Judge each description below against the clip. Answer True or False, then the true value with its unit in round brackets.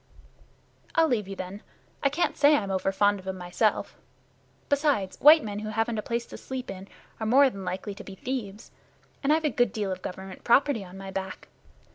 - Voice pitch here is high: True (210 Hz)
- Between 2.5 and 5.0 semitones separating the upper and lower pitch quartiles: False (5.4 semitones)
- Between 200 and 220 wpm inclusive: True (205 wpm)